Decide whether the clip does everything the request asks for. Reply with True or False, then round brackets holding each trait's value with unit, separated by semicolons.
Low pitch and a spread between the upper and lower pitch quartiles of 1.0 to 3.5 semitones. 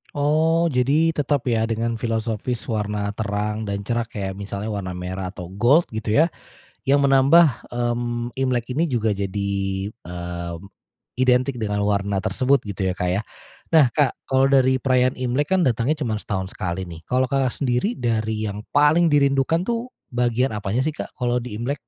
False (120 Hz; 4.9 semitones)